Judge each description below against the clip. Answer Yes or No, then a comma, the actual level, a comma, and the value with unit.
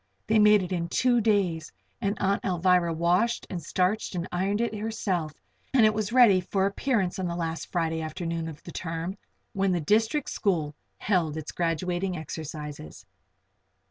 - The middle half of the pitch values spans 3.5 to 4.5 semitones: Yes, average, 3.8 semitones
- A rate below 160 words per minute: No, average, 165 wpm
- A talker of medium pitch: Yes, medium, 180 Hz